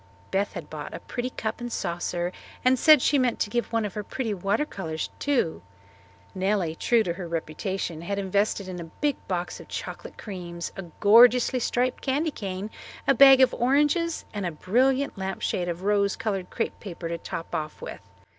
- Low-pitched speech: No, high, 205 Hz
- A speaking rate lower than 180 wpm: No, average, 185 wpm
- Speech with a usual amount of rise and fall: No, wide, 5.7 semitones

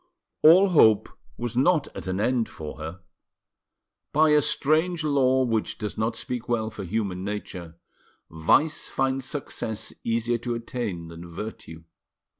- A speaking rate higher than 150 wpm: No, average, 140 wpm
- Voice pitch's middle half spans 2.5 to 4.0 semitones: No, wide, 5.5 semitones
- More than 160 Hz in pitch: No, low, 115 Hz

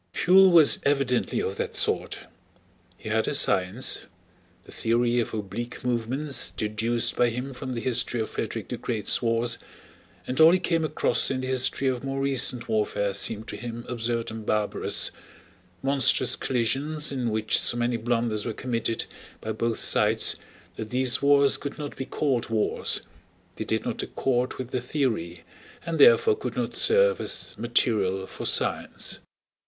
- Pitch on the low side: Yes, low, 120 Hz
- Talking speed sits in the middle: Yes, average, 160 wpm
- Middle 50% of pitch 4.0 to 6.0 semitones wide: No, average, 3.2 semitones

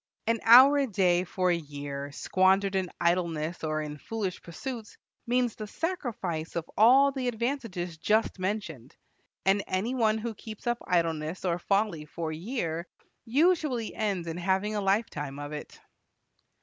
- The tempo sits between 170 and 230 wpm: No, average, 155 wpm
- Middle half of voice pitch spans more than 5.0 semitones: Yes, wide, 5.4 semitones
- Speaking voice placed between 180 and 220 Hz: Yes, high, 190 Hz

